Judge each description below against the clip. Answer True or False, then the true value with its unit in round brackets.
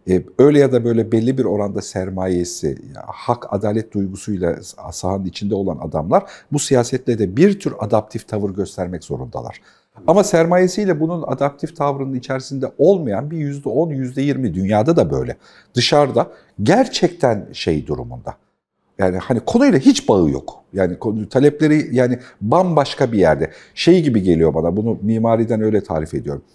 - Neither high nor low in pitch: False (120 Hz)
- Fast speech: True (145 wpm)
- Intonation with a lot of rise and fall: True (6.4 semitones)